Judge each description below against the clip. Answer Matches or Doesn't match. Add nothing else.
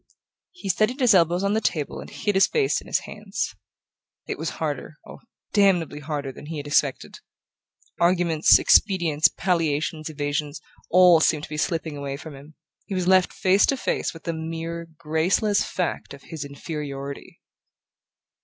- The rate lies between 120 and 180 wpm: Matches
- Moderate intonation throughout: Matches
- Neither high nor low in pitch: Matches